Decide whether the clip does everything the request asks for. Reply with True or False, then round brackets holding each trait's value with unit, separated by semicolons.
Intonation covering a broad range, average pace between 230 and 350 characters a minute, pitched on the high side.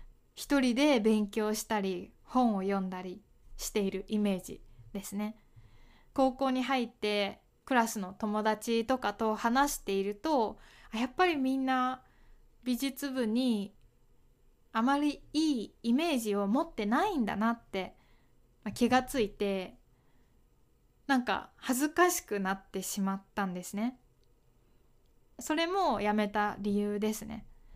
False (4.4 semitones; 240 characters per minute; 220 Hz)